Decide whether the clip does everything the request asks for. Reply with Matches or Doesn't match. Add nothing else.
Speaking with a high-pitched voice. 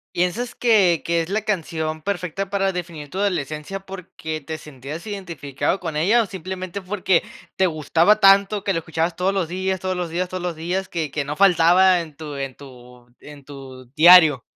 Doesn't match